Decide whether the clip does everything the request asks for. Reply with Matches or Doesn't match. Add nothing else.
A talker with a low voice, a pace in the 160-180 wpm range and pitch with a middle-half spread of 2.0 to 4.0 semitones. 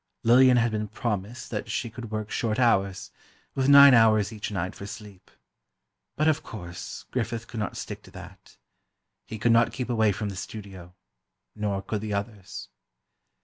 Matches